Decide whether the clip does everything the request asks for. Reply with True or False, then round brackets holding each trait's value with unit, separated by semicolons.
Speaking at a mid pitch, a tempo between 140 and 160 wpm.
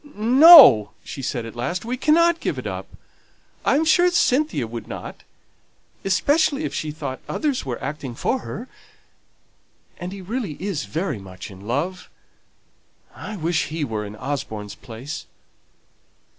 True (165 Hz; 145 wpm)